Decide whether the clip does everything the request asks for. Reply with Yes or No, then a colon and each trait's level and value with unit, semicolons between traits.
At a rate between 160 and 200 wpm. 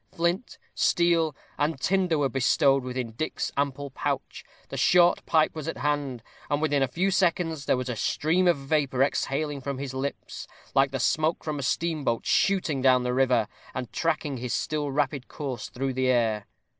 Yes: average, 180 wpm